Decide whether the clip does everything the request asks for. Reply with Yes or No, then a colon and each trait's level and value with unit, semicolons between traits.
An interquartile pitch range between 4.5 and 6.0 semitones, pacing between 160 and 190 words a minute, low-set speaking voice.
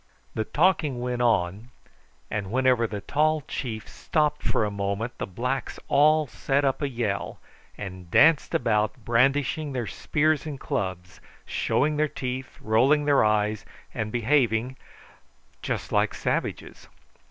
No: average, 5.2 semitones; slow, 135 wpm; low, 125 Hz